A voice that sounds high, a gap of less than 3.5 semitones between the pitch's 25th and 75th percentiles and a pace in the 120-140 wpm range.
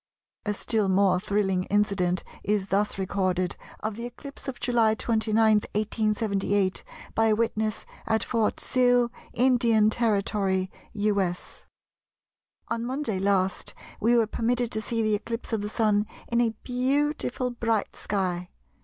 Yes: high, 215 Hz; average, 2.8 semitones; slow, 135 wpm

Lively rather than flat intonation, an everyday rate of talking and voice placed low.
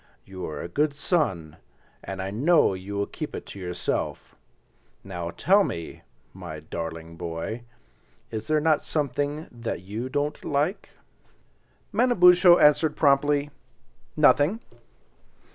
No: wide, 8.7 semitones; slow, 120 wpm; low, 130 Hz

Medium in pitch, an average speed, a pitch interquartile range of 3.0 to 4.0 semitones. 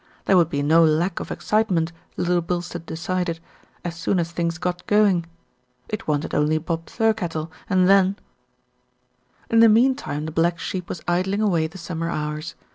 No: medium, 175 Hz; average, 170 wpm; narrow, 2.6 semitones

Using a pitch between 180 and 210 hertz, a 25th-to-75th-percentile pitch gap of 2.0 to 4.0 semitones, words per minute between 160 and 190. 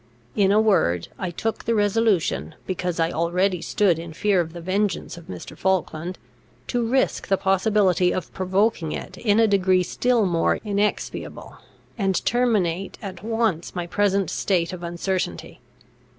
No: high, 190 Hz; average, 3.2 semitones; average, 150 wpm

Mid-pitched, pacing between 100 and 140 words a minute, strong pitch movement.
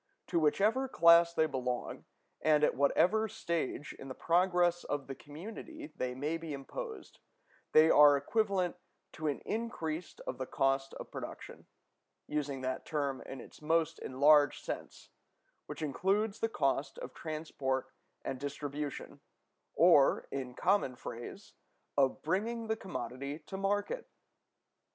Yes: medium, 155 Hz; slow, 135 wpm; wide, 5.7 semitones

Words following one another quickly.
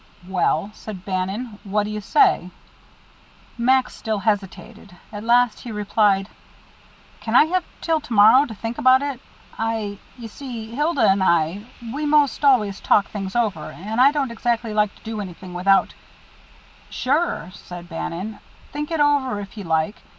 No: average, 165 wpm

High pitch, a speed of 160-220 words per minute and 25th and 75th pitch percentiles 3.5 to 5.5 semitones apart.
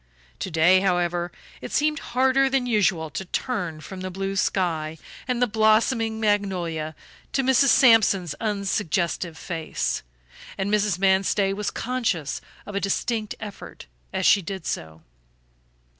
No: high, 195 Hz; slow, 135 wpm; average, 4.2 semitones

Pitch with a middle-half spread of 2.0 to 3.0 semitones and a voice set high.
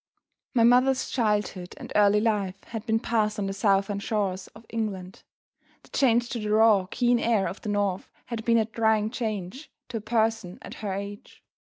Yes: narrow, 2.4 semitones; high, 215 Hz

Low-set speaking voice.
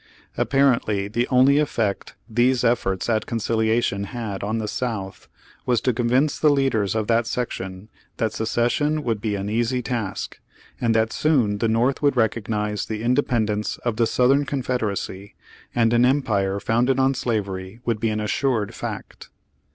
Yes: low, 115 Hz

